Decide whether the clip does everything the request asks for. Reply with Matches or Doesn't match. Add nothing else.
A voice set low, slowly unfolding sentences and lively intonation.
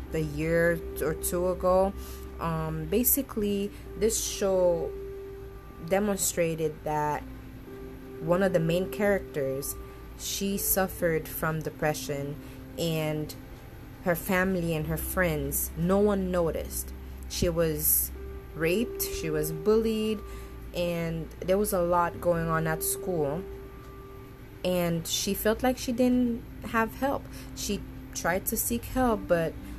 Doesn't match